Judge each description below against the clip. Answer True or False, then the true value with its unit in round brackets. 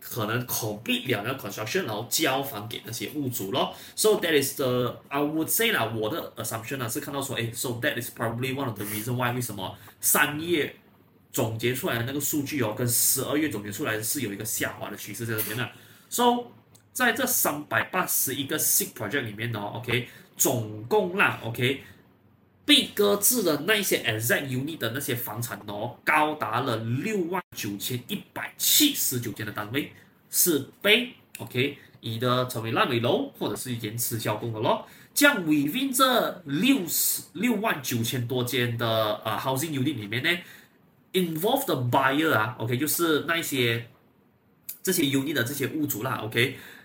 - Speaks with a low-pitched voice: True (125 Hz)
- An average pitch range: True (5.0 semitones)